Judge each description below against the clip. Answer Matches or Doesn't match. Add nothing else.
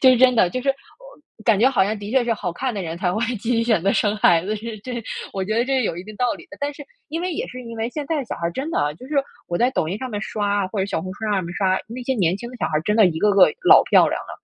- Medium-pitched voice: Doesn't match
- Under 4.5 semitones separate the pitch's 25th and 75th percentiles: Doesn't match